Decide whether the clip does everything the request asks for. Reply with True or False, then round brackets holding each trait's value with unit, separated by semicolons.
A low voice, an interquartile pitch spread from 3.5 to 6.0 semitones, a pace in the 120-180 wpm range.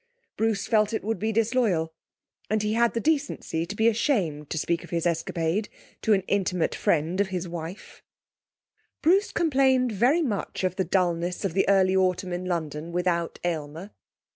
False (190 Hz; 4.5 semitones; 170 wpm)